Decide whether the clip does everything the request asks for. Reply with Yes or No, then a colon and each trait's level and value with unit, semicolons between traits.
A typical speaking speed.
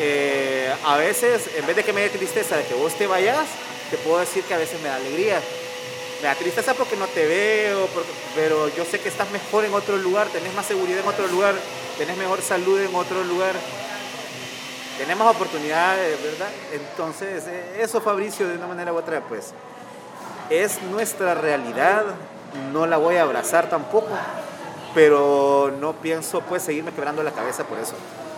Yes: average, 180 wpm